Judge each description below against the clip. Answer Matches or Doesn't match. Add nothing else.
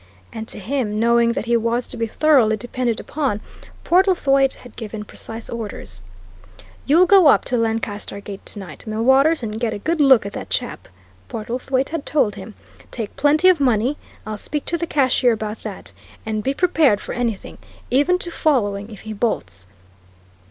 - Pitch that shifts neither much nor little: Matches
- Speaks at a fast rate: Doesn't match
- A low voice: Doesn't match